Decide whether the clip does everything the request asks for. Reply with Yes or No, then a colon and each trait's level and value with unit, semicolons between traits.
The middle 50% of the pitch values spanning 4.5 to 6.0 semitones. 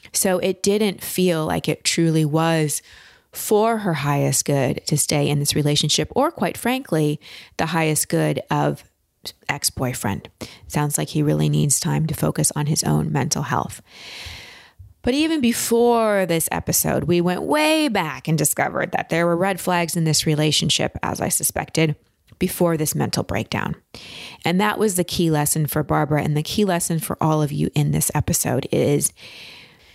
No: average, 3.5 semitones